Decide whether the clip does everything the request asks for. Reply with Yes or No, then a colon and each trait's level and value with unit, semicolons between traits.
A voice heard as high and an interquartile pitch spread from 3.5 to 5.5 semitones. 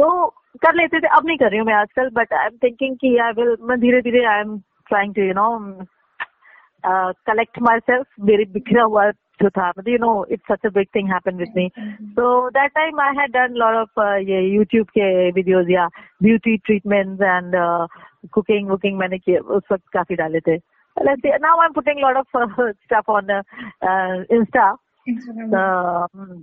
Yes: high, 215 Hz; average, 4.2 semitones